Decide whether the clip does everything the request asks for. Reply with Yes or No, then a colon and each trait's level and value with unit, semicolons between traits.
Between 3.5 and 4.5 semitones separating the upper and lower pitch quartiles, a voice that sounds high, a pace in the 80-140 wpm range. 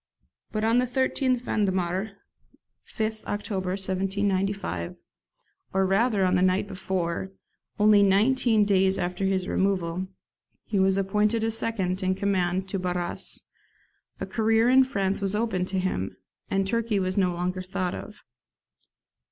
No: narrow, 2.4 semitones; high, 195 Hz; slow, 135 wpm